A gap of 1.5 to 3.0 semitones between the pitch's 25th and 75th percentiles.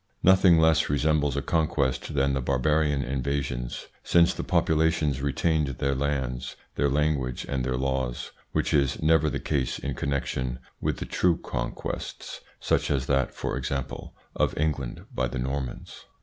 Yes: average, 2.7 semitones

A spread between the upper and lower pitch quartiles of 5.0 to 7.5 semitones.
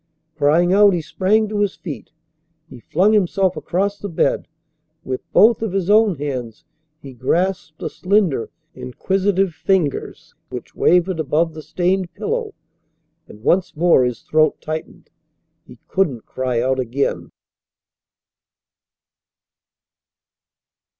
Yes: wide, 5.4 semitones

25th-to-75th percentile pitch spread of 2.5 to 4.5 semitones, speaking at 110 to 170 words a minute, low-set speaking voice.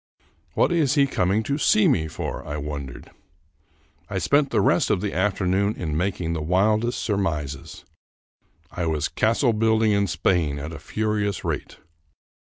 No: average, 5.3 semitones; average, 155 wpm; low, 100 Hz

